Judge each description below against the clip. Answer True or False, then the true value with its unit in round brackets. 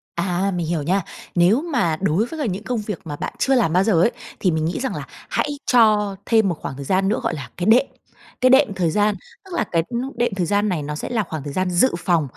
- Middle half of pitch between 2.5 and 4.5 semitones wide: False (5.0 semitones)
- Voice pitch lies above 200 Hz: False (195 Hz)